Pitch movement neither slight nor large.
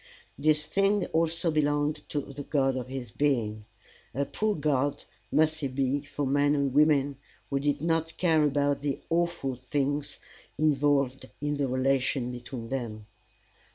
No: narrow, 2.2 semitones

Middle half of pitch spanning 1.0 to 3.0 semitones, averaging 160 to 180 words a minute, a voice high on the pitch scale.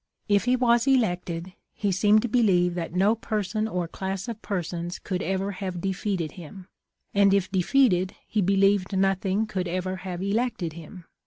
Yes: average, 2.7 semitones; average, 165 wpm; high, 195 Hz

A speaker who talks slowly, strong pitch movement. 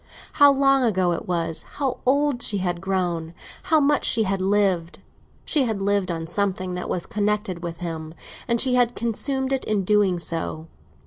No: average, 170 wpm; wide, 5.8 semitones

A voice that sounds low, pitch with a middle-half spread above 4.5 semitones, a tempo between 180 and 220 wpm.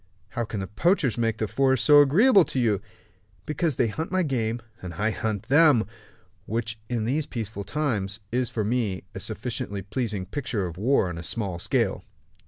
Yes: low, 115 Hz; average, 5.1 semitones; average, 185 wpm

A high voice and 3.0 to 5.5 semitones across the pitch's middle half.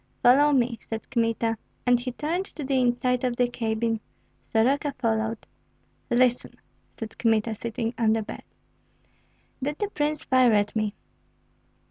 No: high, 240 Hz; narrow, 2.6 semitones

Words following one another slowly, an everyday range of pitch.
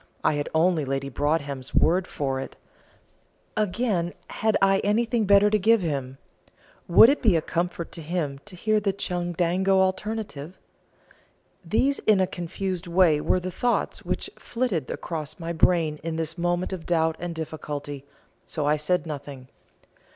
No: average, 155 wpm; average, 4.2 semitones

